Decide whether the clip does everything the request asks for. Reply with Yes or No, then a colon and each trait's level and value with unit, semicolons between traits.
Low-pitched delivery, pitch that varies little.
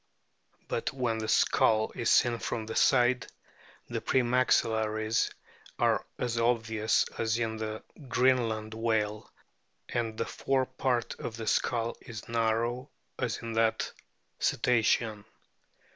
Yes: low, 115 Hz; narrow, 1.6 semitones